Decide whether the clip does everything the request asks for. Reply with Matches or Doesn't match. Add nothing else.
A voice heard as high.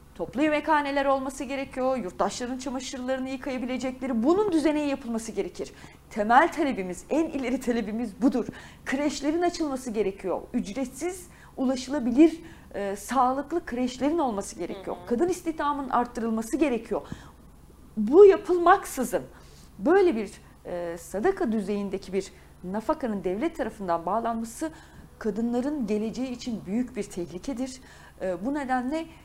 Matches